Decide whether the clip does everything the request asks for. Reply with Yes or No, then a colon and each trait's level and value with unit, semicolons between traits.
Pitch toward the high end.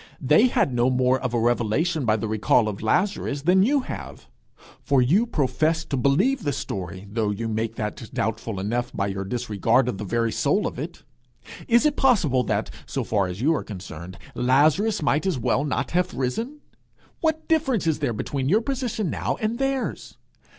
No: low, 130 Hz